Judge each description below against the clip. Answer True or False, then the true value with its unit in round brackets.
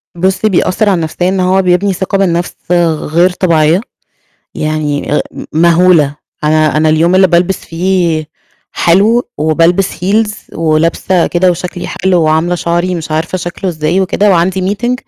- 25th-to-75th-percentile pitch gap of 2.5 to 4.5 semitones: True (2.8 semitones)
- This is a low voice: False (175 Hz)